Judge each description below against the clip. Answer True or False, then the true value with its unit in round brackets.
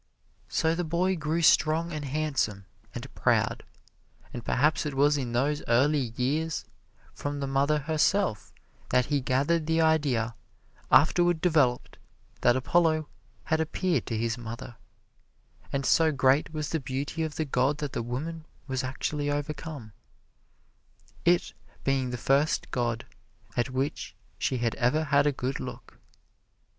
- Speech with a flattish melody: False (3.5 semitones)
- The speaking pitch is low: False (145 Hz)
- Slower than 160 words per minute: True (145 wpm)